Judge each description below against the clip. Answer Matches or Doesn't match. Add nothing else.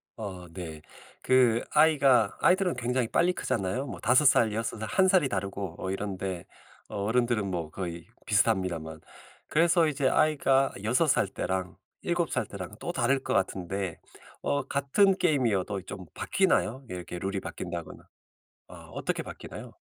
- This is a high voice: Doesn't match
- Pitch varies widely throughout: Matches